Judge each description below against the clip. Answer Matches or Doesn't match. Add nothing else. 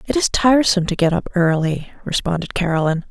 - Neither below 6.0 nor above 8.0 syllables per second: Matches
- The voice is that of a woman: Matches